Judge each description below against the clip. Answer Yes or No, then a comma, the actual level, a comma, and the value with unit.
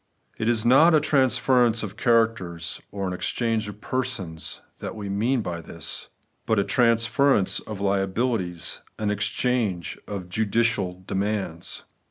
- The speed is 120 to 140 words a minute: Yes, slow, 135 wpm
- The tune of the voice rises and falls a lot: No, average, 3.8 semitones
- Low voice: Yes, low, 110 Hz